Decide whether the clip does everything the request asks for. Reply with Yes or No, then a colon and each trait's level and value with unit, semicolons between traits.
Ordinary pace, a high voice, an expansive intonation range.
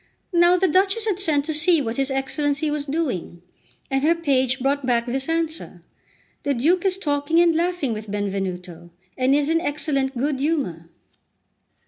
No: average, 165 wpm; very high, 285 Hz; average, 4.4 semitones